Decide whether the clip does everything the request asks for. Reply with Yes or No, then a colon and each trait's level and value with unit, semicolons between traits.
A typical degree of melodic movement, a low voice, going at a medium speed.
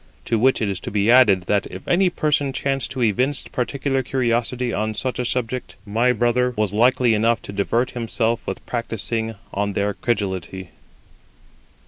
Yes: average, 3.4 semitones; low, 115 Hz; average, 165 wpm